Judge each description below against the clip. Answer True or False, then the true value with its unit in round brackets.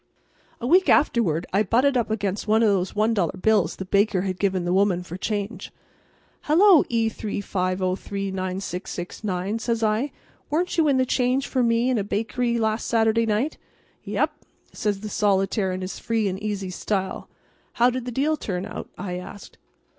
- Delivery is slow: False (170 wpm)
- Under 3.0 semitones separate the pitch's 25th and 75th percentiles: False (3.7 semitones)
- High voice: True (210 Hz)